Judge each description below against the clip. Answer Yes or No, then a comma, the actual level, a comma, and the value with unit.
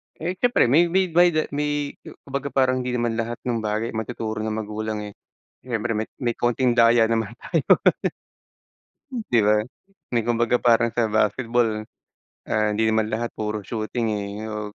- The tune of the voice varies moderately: No, narrow, 2.3 semitones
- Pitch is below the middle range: Yes, low, 115 Hz